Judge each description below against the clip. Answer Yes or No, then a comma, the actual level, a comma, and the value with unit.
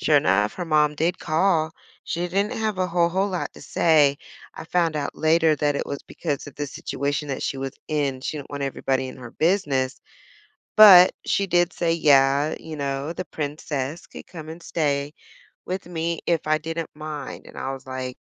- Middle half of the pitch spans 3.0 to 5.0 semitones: Yes, average, 3.4 semitones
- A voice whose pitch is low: No, medium, 155 Hz